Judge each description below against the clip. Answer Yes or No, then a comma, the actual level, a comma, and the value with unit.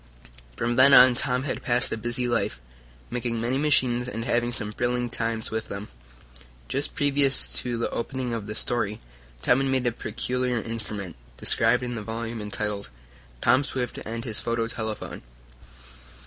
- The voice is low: Yes, low, 120 Hz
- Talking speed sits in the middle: Yes, average, 160 wpm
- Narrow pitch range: Yes, narrow, 2.0 semitones